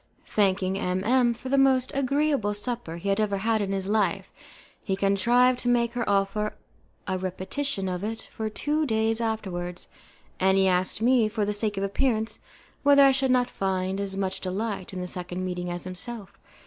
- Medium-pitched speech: No, high, 205 Hz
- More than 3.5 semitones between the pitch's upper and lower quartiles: Yes, average, 4.1 semitones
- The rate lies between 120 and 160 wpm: No, average, 185 wpm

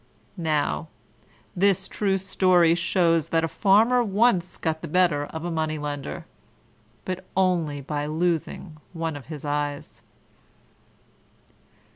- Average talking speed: No, slow, 120 wpm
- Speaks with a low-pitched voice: No, medium, 165 Hz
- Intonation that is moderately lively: Yes, average, 3.6 semitones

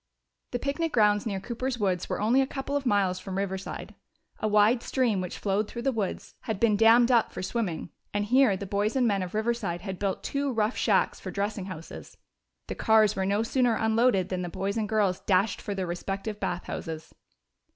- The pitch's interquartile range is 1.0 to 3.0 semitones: No, average, 3.5 semitones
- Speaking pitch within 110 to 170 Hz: No, high, 210 Hz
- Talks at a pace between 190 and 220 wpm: Yes, fast, 205 wpm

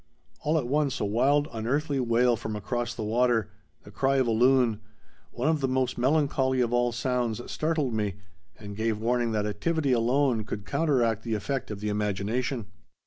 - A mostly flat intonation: No, average, 3.4 semitones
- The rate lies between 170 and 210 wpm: Yes, average, 180 wpm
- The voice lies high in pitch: No, low, 120 Hz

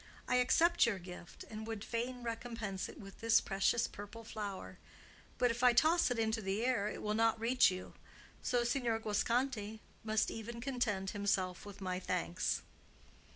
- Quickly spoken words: No, average, 165 wpm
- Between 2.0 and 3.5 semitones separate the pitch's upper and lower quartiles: Yes, average, 3.0 semitones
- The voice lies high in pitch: Yes, high, 225 Hz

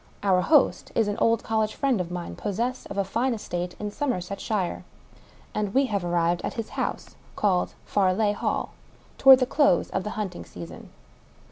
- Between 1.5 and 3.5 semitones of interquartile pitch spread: No, average, 4.1 semitones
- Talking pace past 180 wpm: Yes, average, 190 wpm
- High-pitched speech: Yes, high, 205 Hz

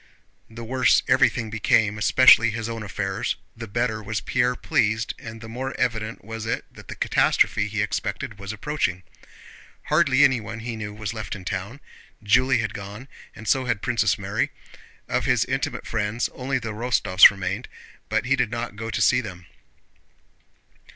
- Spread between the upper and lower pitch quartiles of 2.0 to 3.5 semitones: Yes, average, 2.8 semitones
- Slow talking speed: No, average, 165 wpm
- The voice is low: Yes, low, 110 Hz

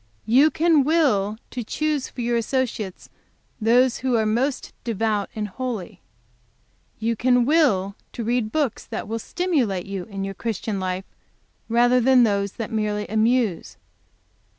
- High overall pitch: Yes, high, 230 Hz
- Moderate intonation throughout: Yes, average, 3.6 semitones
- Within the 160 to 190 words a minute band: No, average, 145 wpm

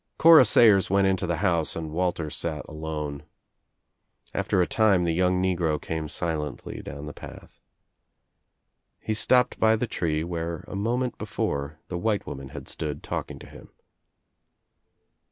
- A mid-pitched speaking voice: No, very low, 85 Hz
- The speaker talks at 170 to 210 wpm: No, average, 150 wpm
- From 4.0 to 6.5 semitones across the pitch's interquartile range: Yes, average, 4.3 semitones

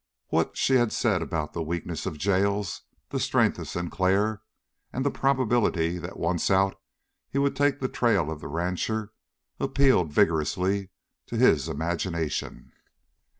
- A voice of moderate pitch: No, very low, 95 Hz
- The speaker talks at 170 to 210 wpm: No, average, 145 wpm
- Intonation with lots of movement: Yes, wide, 5.9 semitones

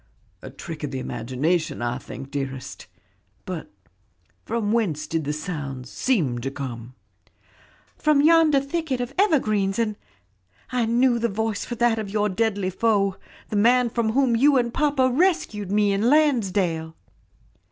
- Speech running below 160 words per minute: Yes, average, 150 wpm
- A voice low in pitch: No, high, 210 Hz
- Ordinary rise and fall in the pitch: No, wide, 7.4 semitones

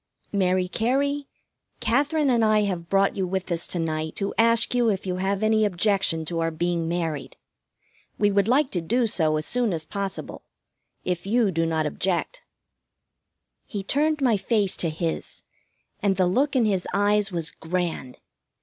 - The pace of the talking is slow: No, average, 170 wpm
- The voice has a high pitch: Yes, high, 195 Hz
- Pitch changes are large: No, average, 4.8 semitones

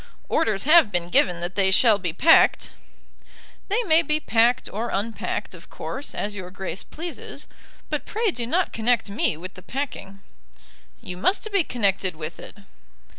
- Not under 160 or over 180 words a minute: Yes, average, 165 wpm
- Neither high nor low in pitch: No, high, 220 Hz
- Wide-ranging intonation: Yes, wide, 8.2 semitones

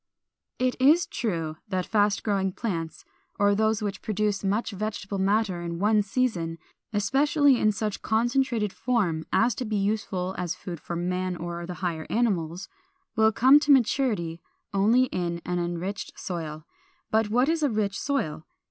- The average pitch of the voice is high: Yes, high, 205 Hz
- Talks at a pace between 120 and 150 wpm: No, average, 160 wpm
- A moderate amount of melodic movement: Yes, average, 4.4 semitones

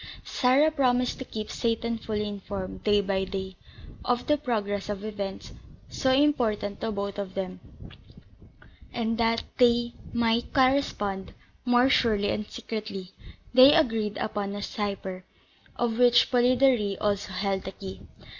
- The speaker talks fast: No, slow, 135 wpm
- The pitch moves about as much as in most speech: Yes, average, 3.4 semitones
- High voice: Yes, high, 215 Hz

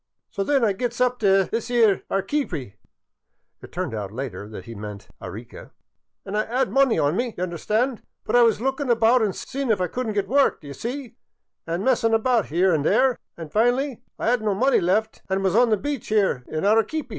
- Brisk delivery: Yes, fast, 230 wpm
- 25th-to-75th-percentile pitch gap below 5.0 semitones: No, wide, 5.4 semitones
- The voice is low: No, high, 220 Hz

